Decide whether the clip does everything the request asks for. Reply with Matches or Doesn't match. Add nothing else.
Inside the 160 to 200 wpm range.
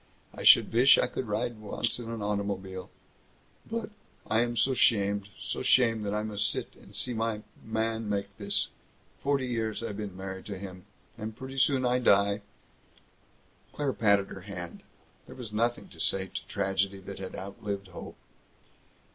Matches